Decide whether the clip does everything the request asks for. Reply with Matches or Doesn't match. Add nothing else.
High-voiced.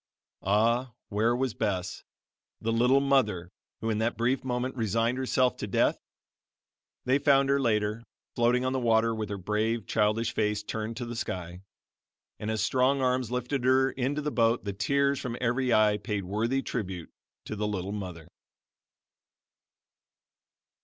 Doesn't match